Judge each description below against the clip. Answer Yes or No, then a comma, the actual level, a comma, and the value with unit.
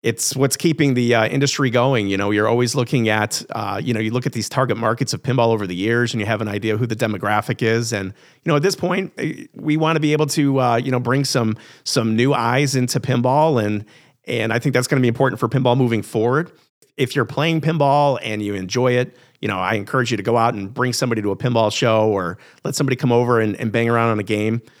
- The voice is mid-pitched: No, low, 120 Hz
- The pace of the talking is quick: Yes, fast, 260 wpm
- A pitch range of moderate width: Yes, average, 3.6 semitones